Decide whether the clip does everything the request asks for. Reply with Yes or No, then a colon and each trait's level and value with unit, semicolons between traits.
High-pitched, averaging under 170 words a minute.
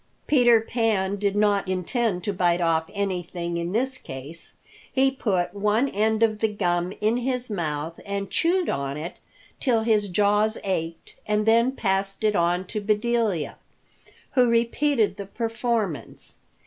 Yes: high, 205 Hz; average, 150 wpm